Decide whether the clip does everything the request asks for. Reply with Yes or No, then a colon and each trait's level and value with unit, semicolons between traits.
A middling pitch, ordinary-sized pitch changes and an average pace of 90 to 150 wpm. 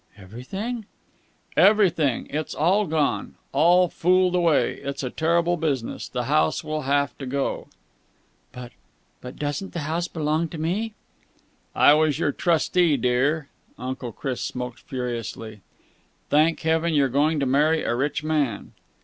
Yes: medium, 150 Hz; average, 4.2 semitones; average, 140 wpm